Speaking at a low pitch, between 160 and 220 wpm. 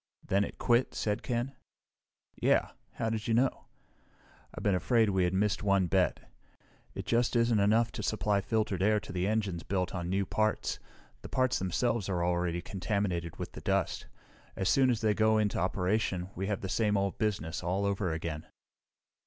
Yes: low, 100 Hz; average, 180 wpm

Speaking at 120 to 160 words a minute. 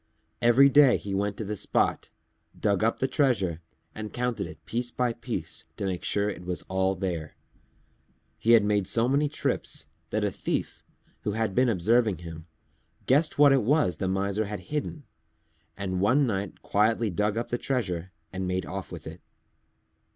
No: average, 175 wpm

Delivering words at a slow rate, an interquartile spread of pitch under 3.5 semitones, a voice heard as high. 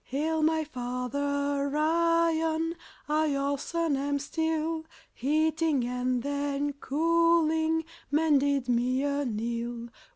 Yes: slow, 100 wpm; average, 2.9 semitones; very high, 285 Hz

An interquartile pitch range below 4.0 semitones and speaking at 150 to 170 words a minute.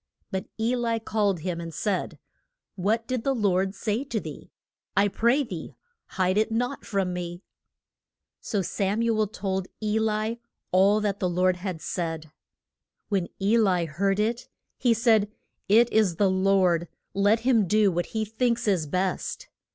Yes: average, 3.3 semitones; average, 165 wpm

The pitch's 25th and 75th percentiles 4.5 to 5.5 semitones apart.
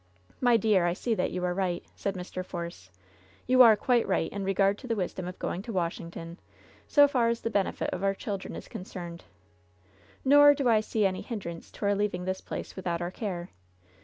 No: average, 4.0 semitones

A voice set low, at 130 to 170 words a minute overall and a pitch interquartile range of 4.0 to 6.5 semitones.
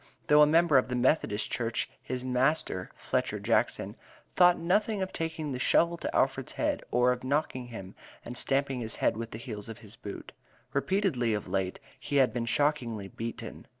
No: low, 125 Hz; average, 185 wpm; average, 4.7 semitones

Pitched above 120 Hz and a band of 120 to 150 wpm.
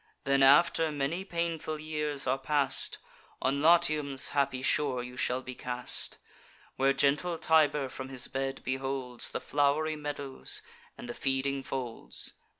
Yes: medium, 140 Hz; average, 140 wpm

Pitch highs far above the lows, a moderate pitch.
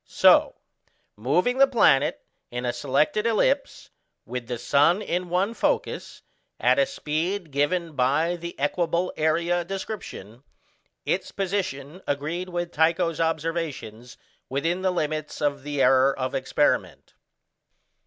No: average, 4.4 semitones; medium, 165 Hz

